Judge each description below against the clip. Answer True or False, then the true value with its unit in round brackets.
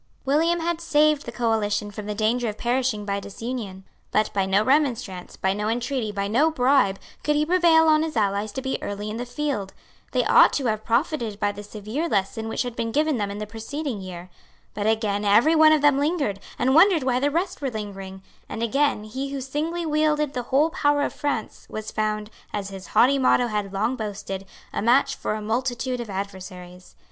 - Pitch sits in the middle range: False (235 Hz)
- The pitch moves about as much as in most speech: False (5.8 semitones)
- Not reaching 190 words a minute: False (205 wpm)